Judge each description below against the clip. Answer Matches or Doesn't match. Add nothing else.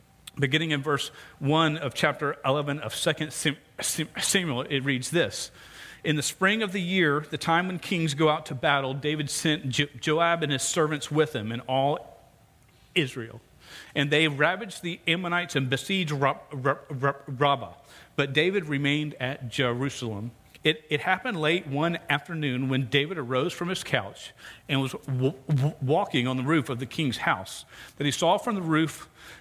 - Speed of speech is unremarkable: Matches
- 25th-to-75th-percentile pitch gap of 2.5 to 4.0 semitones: Matches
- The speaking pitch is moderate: Matches